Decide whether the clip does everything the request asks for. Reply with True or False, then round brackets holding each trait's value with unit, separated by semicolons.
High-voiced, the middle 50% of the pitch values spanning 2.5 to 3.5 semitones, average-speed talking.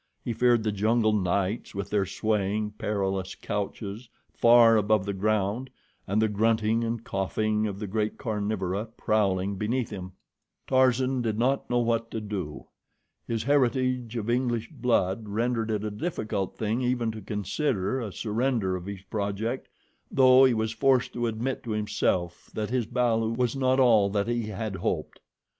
False (110 Hz; 2.9 semitones; 160 wpm)